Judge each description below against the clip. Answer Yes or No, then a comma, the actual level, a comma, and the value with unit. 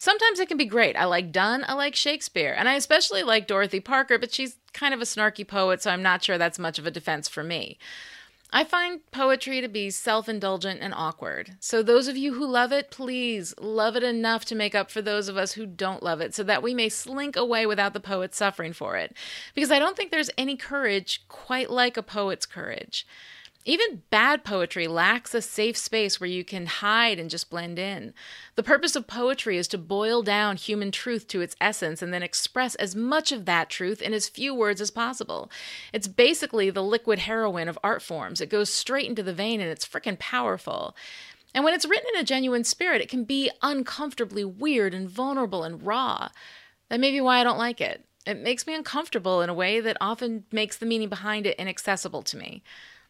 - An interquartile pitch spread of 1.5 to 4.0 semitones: No, average, 4.7 semitones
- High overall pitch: Yes, high, 220 Hz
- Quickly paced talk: Yes, fast, 215 wpm